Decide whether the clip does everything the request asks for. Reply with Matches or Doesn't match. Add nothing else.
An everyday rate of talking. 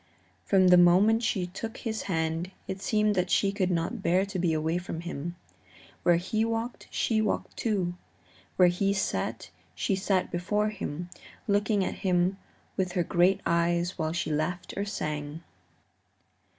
Matches